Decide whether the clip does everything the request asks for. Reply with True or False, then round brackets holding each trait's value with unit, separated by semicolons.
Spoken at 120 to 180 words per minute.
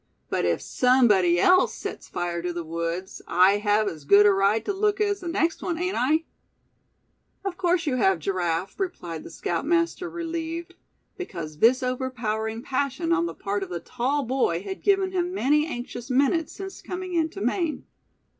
True (175 wpm)